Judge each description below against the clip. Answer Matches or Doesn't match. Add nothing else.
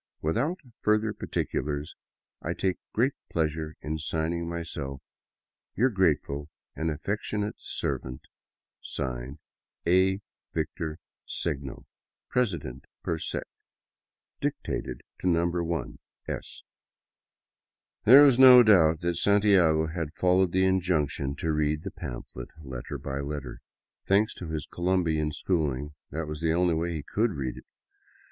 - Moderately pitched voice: Doesn't match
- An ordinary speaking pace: Doesn't match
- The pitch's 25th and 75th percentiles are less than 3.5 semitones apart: Doesn't match